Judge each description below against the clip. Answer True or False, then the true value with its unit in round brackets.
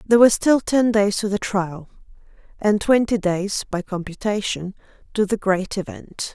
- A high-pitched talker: True (205 Hz)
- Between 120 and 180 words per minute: True (160 wpm)